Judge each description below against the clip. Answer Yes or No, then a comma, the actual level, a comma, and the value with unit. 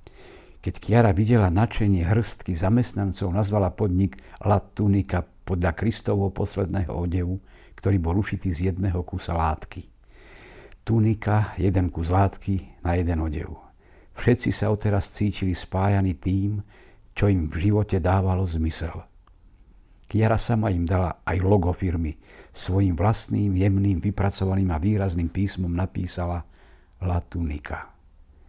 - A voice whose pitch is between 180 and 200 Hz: No, very low, 95 Hz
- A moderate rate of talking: Yes, average, 120 wpm